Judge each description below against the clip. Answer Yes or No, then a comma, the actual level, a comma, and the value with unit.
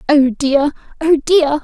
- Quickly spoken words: No, average, 145 wpm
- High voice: Yes, very high, 295 Hz